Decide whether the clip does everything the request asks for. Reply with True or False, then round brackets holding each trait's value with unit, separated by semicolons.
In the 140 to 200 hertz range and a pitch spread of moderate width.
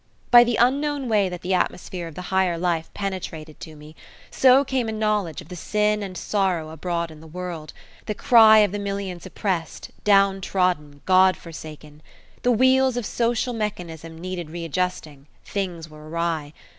True (185 Hz; 4.5 semitones)